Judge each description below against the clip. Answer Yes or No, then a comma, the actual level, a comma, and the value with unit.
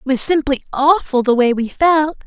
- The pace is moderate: No, fast, 210 wpm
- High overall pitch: Yes, very high, 280 Hz